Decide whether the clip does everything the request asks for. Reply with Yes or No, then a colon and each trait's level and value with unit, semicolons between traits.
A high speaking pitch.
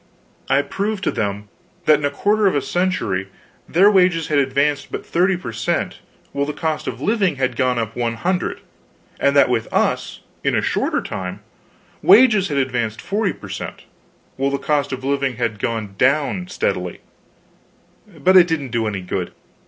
No: medium, 140 Hz